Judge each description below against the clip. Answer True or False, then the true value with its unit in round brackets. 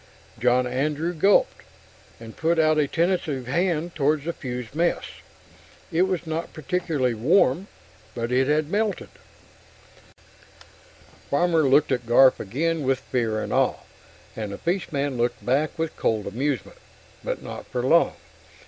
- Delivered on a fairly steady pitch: False (4.9 semitones)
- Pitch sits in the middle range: True (150 Hz)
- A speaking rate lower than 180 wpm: True (140 wpm)